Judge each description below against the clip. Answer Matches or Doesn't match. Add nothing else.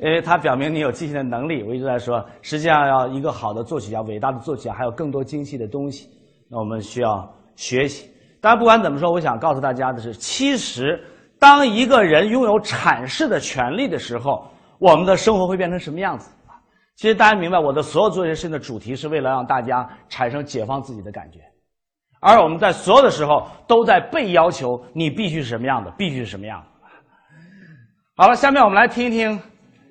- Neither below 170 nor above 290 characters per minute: Doesn't match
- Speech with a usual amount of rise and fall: Doesn't match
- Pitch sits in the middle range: Matches